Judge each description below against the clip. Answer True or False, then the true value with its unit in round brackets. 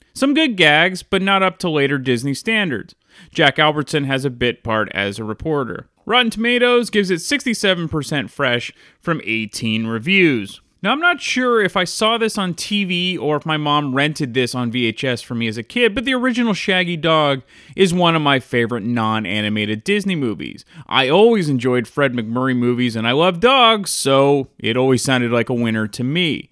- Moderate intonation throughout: False (8.1 semitones)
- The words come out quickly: False (190 wpm)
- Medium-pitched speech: True (145 Hz)